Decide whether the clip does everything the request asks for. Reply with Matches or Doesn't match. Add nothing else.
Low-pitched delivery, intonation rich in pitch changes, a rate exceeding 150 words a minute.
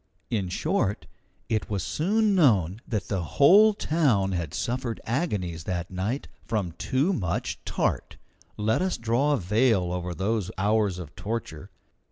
Doesn't match